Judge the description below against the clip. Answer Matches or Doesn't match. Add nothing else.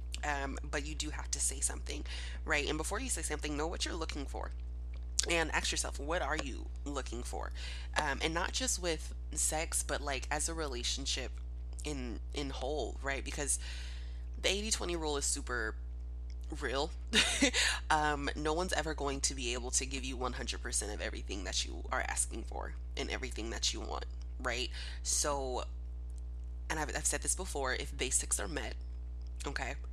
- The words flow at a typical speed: Matches